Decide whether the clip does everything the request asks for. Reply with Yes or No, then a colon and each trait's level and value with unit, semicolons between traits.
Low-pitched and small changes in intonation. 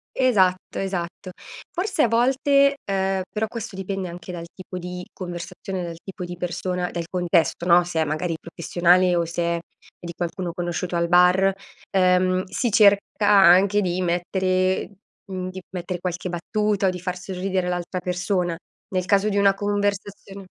No: medium, 185 Hz; narrow, 1.8 semitones